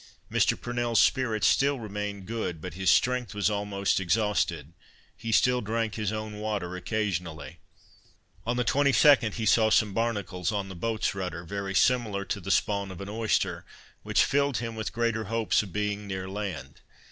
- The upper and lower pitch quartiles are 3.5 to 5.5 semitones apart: No, average, 2.9 semitones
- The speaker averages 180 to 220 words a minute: No, average, 170 wpm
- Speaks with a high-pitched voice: No, low, 105 Hz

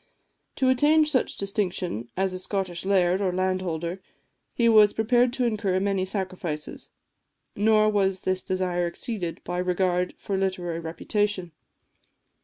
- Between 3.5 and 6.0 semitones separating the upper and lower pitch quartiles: No, narrow, 2.6 semitones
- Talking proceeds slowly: Yes, slow, 130 wpm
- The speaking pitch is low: No, high, 190 Hz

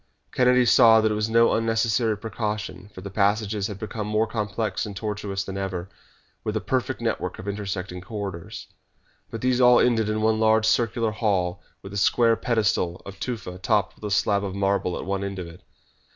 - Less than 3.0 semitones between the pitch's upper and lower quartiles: Yes, narrow, 2.4 semitones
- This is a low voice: Yes, low, 105 Hz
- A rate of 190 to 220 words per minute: Yes, average, 195 wpm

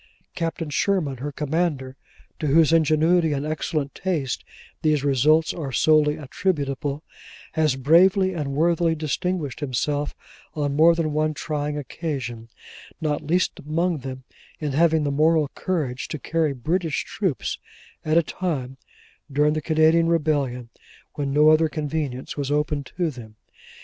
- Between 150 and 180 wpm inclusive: No, average, 140 wpm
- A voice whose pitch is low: No, medium, 150 Hz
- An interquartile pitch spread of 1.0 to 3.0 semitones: Yes, narrow, 2.6 semitones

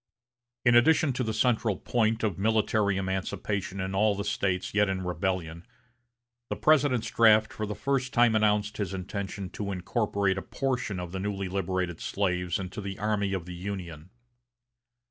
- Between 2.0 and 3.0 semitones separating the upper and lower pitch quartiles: Yes, narrow, 2.6 semitones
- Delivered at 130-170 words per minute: Yes, average, 165 wpm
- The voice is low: Yes, low, 100 Hz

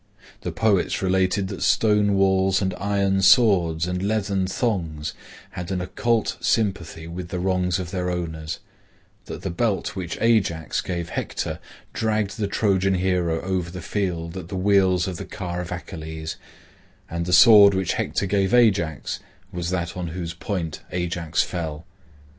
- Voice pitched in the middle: No, very low, 90 Hz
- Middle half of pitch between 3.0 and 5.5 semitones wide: No, narrow, 2.5 semitones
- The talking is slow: No, average, 155 wpm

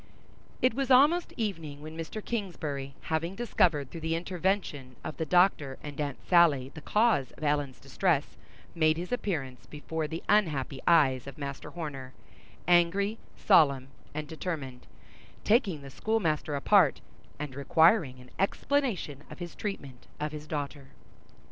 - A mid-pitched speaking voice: Yes, medium, 155 Hz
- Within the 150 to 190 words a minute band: No, average, 140 wpm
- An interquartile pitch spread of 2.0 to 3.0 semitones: No, average, 5.1 semitones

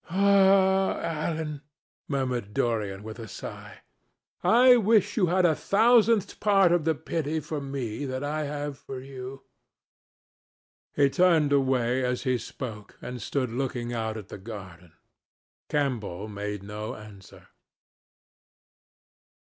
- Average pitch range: No, wide, 6.9 semitones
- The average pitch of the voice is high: No, low, 135 Hz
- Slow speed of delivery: Yes, slow, 125 wpm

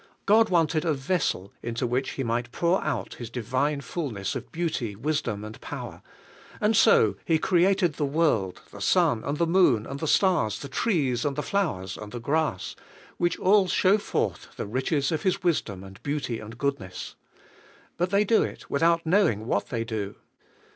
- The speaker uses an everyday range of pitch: No, wide, 7.0 semitones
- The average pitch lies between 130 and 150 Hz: Yes, medium, 140 Hz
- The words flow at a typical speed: Yes, average, 180 wpm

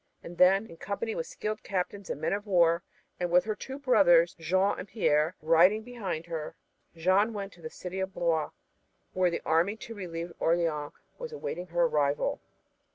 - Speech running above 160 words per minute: Yes, average, 180 wpm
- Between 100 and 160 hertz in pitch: No, medium, 180 Hz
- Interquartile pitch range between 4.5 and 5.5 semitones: No, average, 3.5 semitones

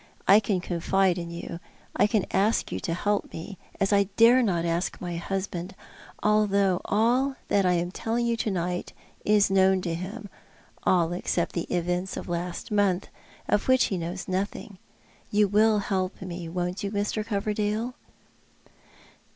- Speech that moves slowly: No, average, 170 wpm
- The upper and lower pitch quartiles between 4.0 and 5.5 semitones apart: No, average, 2.8 semitones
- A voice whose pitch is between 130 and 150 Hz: No, high, 195 Hz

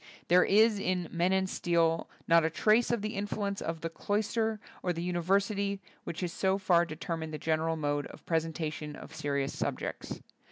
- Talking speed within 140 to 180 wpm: No, average, 190 wpm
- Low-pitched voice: No, medium, 175 Hz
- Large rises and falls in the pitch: No, average, 3.6 semitones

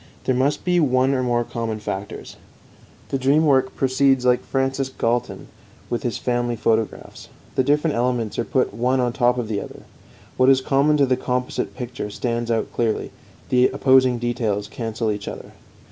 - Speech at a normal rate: Yes, average, 175 wpm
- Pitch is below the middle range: Yes, low, 125 Hz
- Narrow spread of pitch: Yes, narrow, 2.3 semitones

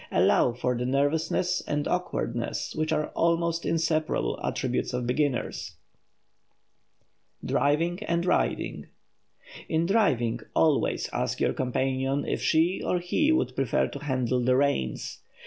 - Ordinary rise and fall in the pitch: Yes, average, 4.6 semitones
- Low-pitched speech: No, medium, 150 Hz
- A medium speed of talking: No, slow, 130 wpm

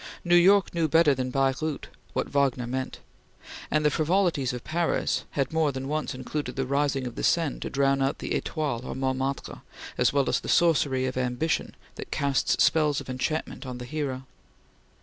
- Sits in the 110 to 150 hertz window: Yes, medium, 140 Hz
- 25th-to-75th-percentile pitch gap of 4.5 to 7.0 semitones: No, average, 3.1 semitones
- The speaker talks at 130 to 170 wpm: No, average, 185 wpm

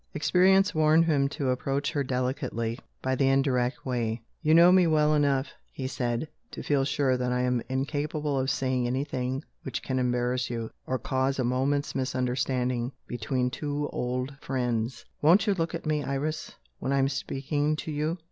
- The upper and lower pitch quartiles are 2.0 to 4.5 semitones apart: Yes, average, 2.8 semitones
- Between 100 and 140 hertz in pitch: Yes, low, 135 Hz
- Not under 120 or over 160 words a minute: No, average, 175 wpm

